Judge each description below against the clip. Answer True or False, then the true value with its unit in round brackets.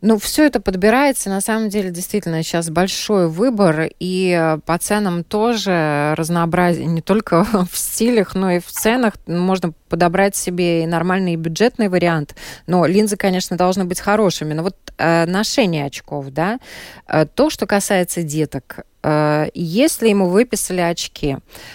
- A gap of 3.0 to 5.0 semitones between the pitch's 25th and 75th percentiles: True (3.9 semitones)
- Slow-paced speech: False (150 wpm)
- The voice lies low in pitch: False (180 Hz)